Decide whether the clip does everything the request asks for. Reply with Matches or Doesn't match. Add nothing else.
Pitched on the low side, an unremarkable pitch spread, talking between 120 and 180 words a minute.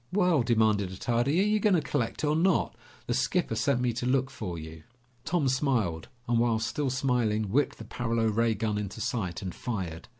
Doesn't match